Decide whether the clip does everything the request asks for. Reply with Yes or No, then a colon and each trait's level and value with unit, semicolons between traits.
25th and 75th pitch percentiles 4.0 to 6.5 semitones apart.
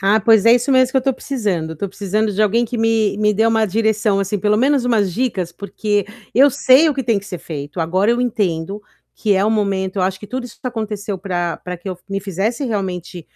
No: average, 3.3 semitones